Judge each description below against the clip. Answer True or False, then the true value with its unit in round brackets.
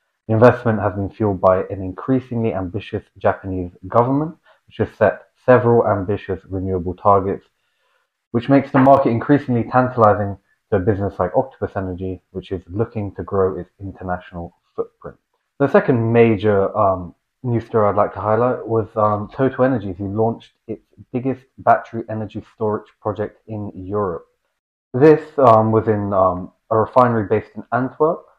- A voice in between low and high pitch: False (105 Hz)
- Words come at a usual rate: True (150 wpm)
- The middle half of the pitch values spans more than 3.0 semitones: True (4.1 semitones)